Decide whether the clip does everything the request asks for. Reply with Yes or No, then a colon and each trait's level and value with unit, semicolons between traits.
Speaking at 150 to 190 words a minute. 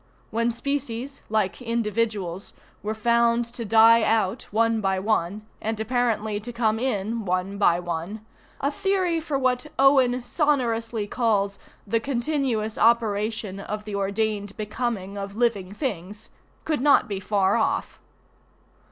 No: slow, 135 wpm